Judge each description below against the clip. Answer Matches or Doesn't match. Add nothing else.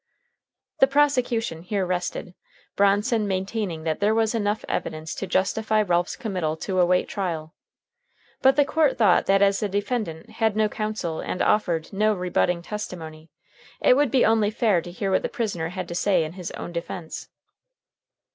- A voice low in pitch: Doesn't match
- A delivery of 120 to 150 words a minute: Doesn't match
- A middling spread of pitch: Matches